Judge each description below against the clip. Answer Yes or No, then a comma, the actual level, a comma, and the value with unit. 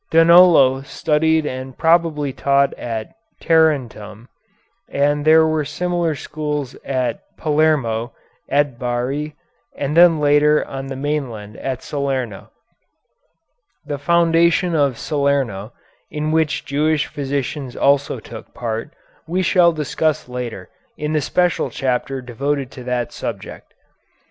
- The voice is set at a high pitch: No, medium, 145 Hz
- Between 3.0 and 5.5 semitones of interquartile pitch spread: Yes, average, 3.4 semitones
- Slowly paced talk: Yes, slow, 115 wpm